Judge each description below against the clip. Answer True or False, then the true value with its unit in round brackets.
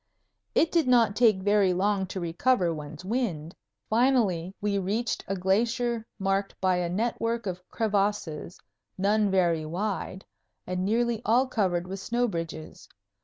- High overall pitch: True (200 Hz)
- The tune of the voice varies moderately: True (3.9 semitones)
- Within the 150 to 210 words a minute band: False (140 wpm)